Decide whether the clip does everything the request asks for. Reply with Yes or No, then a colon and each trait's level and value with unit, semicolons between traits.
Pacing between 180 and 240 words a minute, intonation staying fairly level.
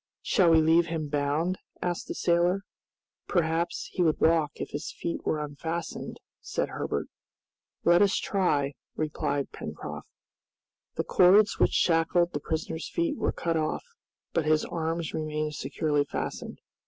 No: average, 140 wpm; narrow, 2.1 semitones